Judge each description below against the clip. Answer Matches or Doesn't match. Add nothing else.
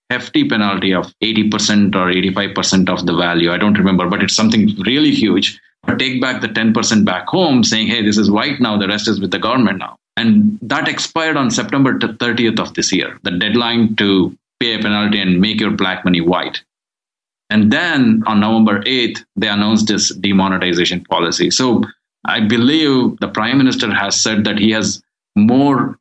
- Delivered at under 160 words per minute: Doesn't match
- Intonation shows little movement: Doesn't match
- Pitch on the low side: Matches